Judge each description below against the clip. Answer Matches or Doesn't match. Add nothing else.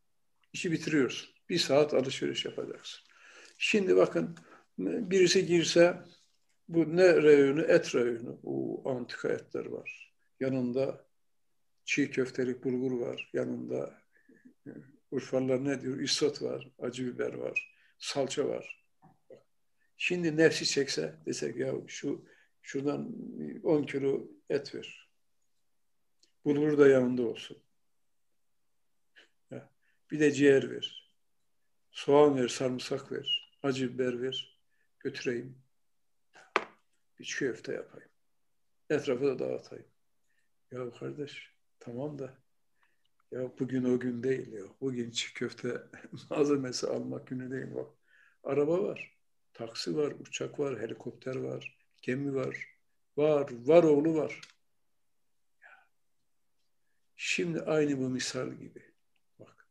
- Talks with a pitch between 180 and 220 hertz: Doesn't match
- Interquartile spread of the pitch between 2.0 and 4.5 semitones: Matches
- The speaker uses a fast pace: Doesn't match